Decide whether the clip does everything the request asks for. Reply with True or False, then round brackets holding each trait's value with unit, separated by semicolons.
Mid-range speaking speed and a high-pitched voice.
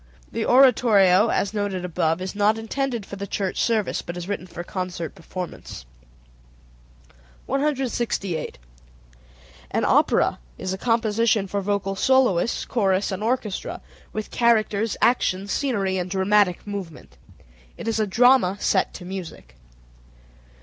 False (130 wpm; 200 Hz)